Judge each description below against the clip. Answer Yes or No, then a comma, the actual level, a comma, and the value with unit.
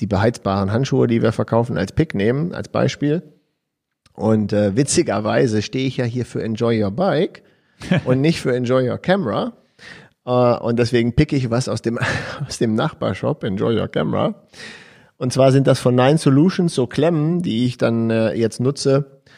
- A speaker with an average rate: Yes, average, 175 wpm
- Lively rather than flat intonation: No, average, 3.5 semitones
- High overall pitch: No, low, 125 Hz